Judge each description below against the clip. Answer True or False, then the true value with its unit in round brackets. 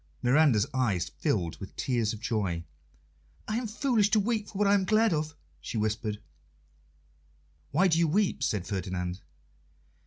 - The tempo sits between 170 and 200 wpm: False (155 wpm)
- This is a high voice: False (130 Hz)